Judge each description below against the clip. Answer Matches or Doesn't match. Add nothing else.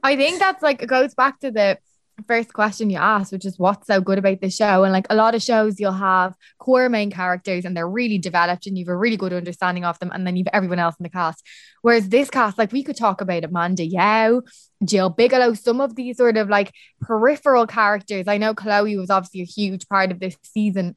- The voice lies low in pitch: Doesn't match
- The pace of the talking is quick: Matches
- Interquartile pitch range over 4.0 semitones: Doesn't match